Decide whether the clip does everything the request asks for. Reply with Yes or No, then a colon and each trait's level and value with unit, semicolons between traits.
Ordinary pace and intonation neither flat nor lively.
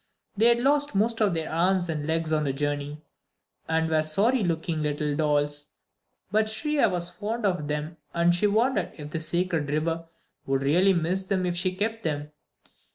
Yes: average, 185 wpm; average, 4.8 semitones